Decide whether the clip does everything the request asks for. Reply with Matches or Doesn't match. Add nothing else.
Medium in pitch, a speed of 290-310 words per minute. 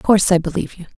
Matches